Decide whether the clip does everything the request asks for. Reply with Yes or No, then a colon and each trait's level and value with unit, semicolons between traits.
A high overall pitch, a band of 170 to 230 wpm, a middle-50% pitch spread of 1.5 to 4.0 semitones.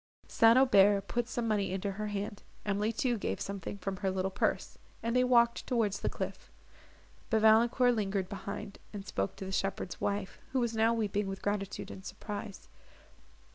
Yes: high, 205 Hz; average, 175 wpm; average, 2.8 semitones